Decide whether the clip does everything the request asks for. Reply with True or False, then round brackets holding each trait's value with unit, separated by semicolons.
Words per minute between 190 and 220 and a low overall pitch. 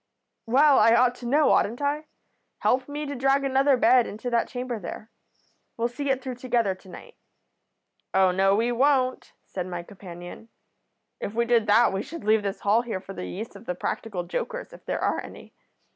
False (195 wpm; 235 Hz)